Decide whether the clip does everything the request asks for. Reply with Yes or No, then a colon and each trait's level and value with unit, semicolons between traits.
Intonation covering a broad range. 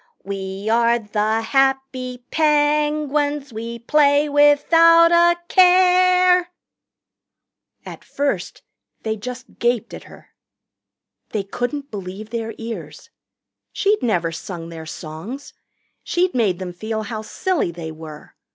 Yes: wide, 6.1 semitones